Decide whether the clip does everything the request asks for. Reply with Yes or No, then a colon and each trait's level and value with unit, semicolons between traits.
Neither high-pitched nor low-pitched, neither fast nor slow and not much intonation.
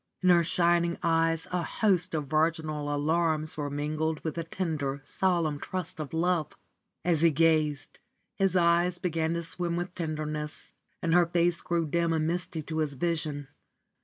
Yes: medium, 165 Hz; average, 160 wpm; narrow, 2.0 semitones